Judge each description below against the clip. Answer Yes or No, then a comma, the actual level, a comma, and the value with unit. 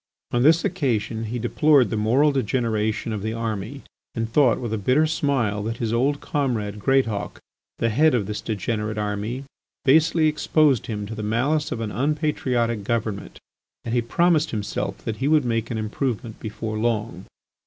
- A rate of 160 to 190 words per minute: Yes, average, 170 wpm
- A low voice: Yes, low, 115 Hz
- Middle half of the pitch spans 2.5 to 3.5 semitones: No, average, 4.4 semitones